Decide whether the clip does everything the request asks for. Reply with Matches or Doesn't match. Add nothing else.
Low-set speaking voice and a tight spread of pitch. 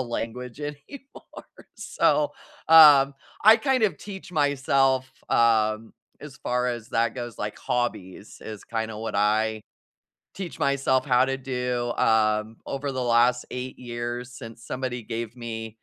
Doesn't match